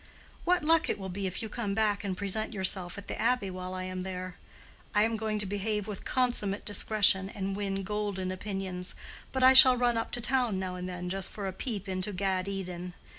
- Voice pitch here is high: Yes, high, 200 Hz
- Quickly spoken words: Yes, fast, 220 wpm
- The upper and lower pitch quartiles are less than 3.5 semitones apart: Yes, average, 2.7 semitones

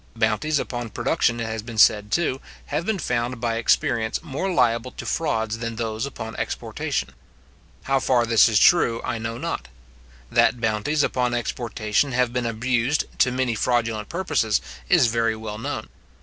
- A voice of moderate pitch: No, low, 115 Hz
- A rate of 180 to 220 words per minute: No, average, 165 wpm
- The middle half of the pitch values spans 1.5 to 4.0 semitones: Yes, narrow, 2.4 semitones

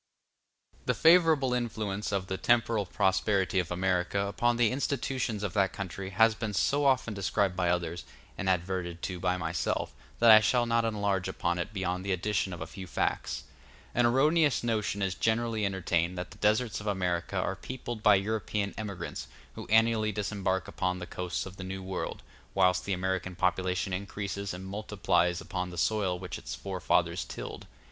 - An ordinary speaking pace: Yes, average, 175 wpm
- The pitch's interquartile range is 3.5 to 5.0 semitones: No, average, 2.9 semitones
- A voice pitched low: Yes, low, 100 Hz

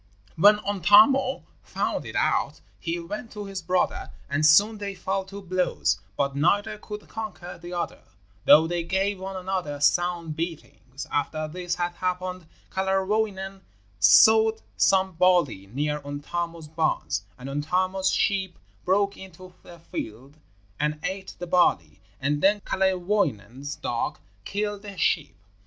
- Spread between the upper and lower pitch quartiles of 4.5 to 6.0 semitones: No, average, 4.1 semitones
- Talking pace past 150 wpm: No, slow, 135 wpm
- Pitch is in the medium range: Yes, medium, 180 Hz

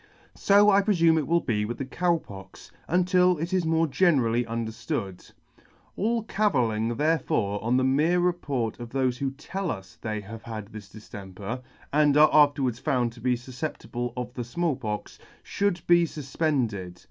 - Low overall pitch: Yes, low, 130 Hz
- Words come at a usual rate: Yes, average, 170 wpm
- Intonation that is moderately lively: No, wide, 6.5 semitones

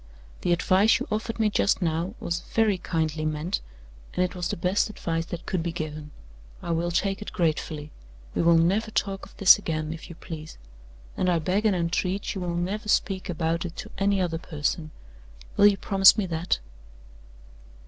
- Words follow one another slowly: No, average, 190 wpm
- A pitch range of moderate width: Yes, average, 3.1 semitones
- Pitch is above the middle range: No, medium, 175 Hz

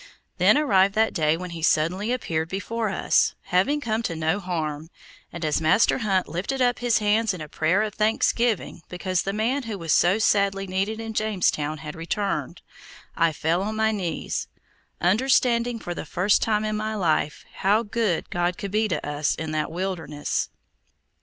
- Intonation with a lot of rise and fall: No, average, 4.7 semitones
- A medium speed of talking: Yes, average, 180 wpm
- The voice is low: No, high, 195 Hz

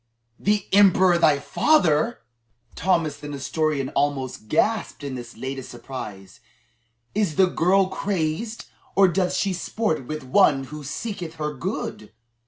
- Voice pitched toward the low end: No, medium, 155 Hz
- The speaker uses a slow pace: Yes, slow, 130 wpm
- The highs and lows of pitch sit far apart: Yes, wide, 5.7 semitones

